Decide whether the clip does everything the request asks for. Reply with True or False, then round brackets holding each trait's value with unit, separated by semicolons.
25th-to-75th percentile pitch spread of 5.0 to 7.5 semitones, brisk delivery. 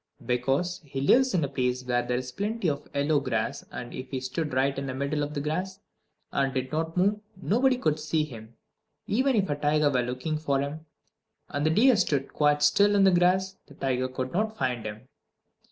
True (5.6 semitones; 210 wpm)